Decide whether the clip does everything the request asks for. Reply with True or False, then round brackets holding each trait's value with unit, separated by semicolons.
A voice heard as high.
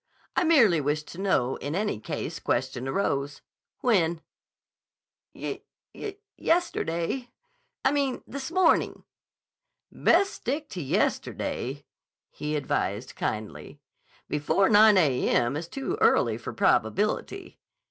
False (170 Hz)